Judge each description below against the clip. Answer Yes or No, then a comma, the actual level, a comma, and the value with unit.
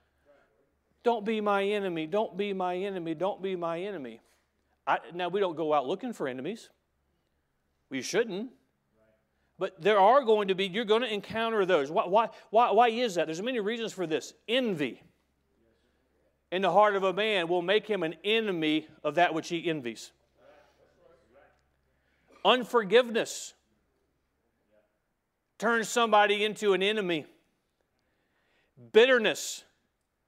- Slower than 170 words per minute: Yes, slow, 135 wpm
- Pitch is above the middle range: Yes, high, 195 Hz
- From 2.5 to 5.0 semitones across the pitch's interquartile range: No, wide, 5.5 semitones